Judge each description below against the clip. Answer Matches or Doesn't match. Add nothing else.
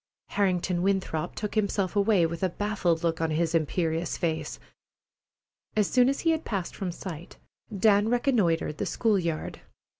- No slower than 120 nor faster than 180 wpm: Matches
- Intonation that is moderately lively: Matches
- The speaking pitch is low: Doesn't match